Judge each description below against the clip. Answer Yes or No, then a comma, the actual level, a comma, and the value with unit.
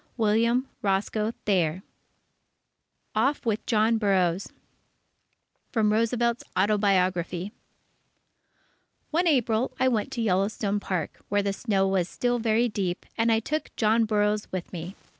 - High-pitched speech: Yes, high, 210 Hz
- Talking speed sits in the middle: No, slow, 120 wpm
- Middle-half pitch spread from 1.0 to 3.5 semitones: Yes, average, 3.1 semitones